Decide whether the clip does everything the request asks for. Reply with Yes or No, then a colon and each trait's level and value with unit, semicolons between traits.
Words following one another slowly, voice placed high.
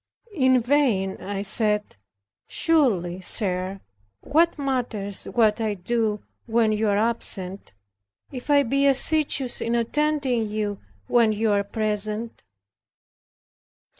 Yes: slow, 115 wpm; high, 225 Hz